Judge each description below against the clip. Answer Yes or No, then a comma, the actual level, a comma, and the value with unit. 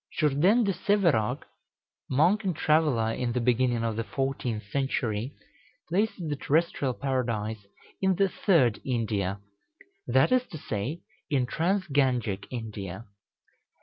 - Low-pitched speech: Yes, low, 130 Hz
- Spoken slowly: Yes, slow, 125 wpm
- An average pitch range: No, wide, 6.5 semitones